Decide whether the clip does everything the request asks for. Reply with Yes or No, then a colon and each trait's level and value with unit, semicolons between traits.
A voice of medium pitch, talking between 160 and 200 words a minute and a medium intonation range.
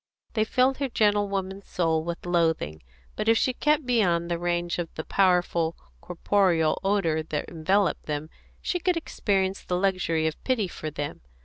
Yes: medium, 180 Hz; average, 165 wpm; average, 3.9 semitones